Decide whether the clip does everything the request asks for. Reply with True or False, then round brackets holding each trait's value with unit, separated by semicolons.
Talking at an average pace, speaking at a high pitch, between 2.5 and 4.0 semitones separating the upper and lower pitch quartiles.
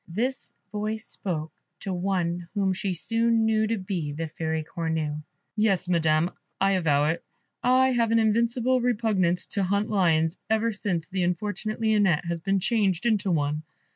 False (160 wpm; 195 Hz; 4.6 semitones)